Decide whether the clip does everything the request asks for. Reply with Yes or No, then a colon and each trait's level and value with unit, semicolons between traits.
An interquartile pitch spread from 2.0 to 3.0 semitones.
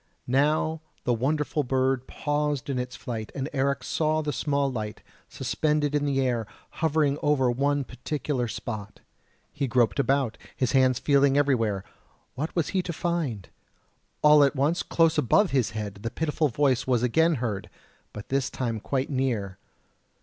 No: average, 3.4 semitones